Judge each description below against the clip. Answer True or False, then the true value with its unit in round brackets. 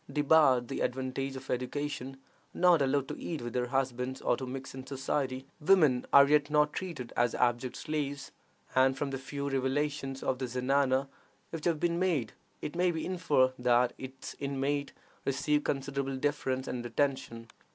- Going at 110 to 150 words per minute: False (165 wpm)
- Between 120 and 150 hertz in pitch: True (135 Hz)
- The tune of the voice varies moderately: False (2.2 semitones)